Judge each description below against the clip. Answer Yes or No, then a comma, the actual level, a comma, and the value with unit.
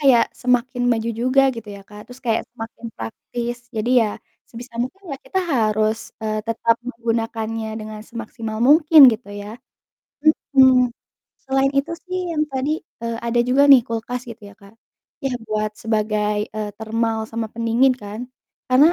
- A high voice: Yes, high, 230 Hz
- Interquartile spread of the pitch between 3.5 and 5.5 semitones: No, average, 2.7 semitones